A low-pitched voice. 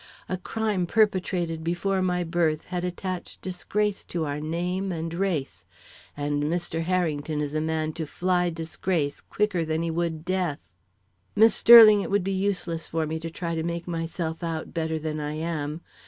No: medium, 170 Hz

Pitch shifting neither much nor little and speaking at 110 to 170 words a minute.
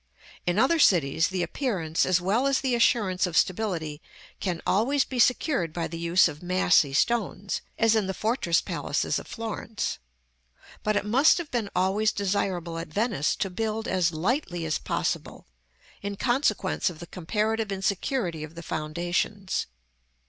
Yes: average, 4.5 semitones; average, 155 wpm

